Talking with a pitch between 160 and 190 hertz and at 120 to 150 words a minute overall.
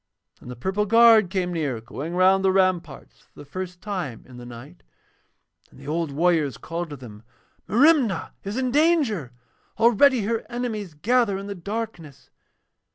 No: medium, 185 Hz; average, 160 wpm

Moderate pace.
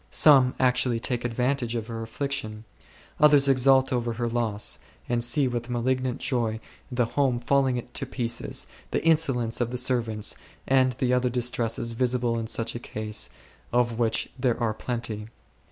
Yes: average, 155 wpm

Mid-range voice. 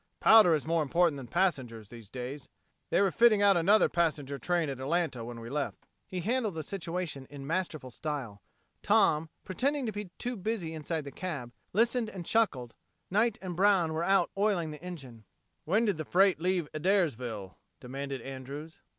Yes: medium, 165 Hz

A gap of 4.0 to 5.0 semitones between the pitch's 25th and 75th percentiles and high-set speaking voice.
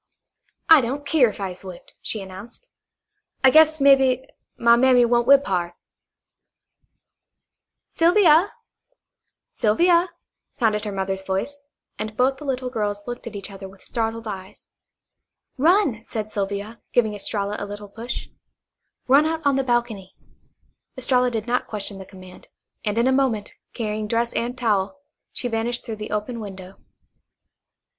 Yes: average, 4.3 semitones; high, 230 Hz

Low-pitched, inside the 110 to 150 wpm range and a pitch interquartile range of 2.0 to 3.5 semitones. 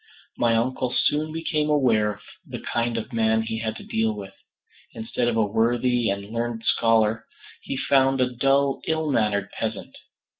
No: low, 115 Hz; average, 165 wpm; average, 3.1 semitones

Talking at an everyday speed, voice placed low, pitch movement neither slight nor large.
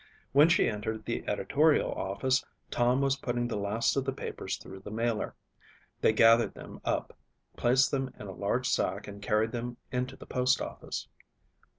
Yes: average, 170 wpm; low, 120 Hz; average, 3.4 semitones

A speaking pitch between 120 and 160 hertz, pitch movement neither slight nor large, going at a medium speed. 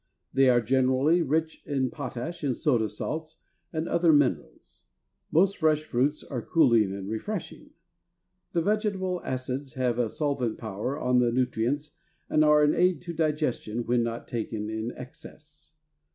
Yes: low, 135 Hz; average, 4.6 semitones; average, 150 wpm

